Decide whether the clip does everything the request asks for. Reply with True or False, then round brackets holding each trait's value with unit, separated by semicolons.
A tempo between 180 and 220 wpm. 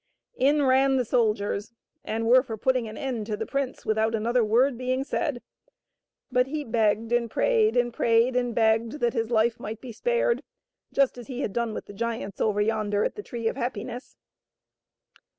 True (190 wpm)